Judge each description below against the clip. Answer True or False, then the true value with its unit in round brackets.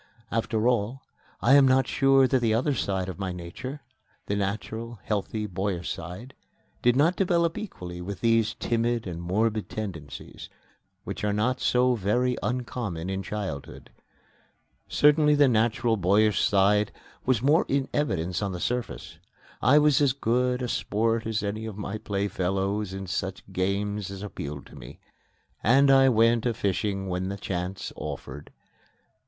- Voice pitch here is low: True (110 Hz)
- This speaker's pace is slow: False (155 wpm)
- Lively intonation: False (4.5 semitones)